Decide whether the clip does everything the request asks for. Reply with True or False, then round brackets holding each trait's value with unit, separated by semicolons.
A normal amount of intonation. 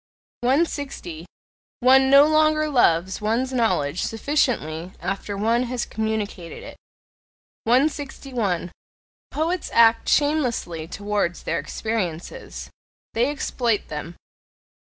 False (6.6 semitones)